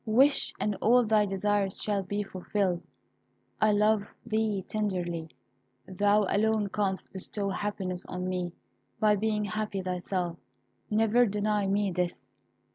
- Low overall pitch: No, high, 205 Hz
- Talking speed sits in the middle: No, slow, 125 wpm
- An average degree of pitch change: No, narrow, 2.3 semitones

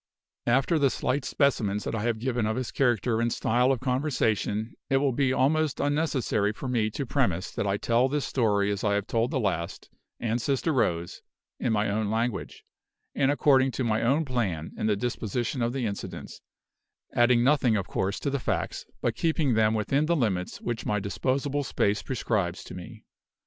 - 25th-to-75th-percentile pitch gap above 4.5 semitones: No, average, 4.1 semitones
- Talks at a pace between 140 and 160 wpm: No, average, 190 wpm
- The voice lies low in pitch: Yes, low, 120 Hz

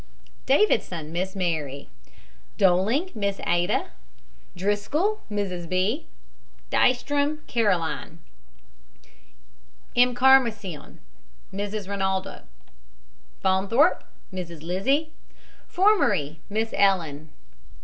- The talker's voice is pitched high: Yes, high, 200 Hz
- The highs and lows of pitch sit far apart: Yes, wide, 5.8 semitones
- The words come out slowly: Yes, slow, 65 wpm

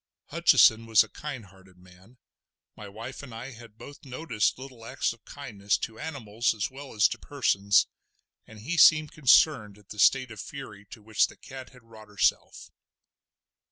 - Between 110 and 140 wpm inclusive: No, average, 165 wpm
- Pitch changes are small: No, average, 4.2 semitones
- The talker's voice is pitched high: No, low, 115 Hz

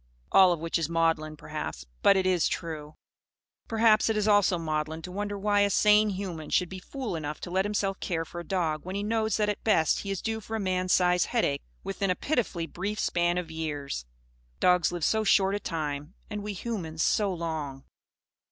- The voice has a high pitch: No, medium, 180 Hz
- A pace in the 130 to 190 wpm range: No, fast, 205 wpm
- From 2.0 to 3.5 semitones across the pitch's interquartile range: No, average, 4.1 semitones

